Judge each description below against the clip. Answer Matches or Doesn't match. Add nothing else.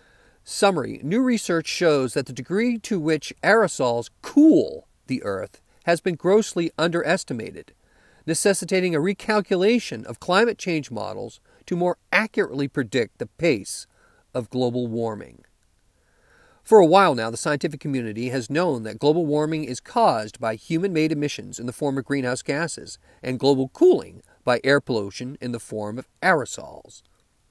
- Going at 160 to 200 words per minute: Doesn't match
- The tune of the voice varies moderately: Doesn't match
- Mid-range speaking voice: Matches